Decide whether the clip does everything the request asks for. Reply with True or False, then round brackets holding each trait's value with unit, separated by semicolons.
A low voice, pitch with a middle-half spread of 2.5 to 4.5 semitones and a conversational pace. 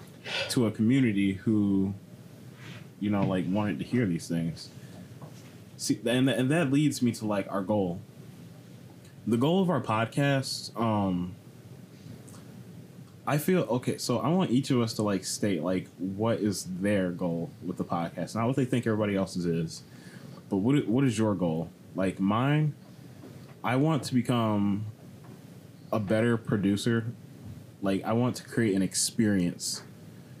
False (110 Hz; 5.2 semitones; 150 wpm)